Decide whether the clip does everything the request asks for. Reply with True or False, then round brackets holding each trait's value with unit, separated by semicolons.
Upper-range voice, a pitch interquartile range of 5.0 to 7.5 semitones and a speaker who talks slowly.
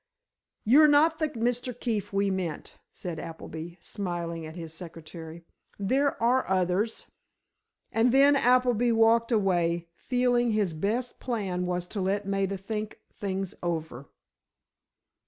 True (200 Hz; 5.6 semitones; 125 wpm)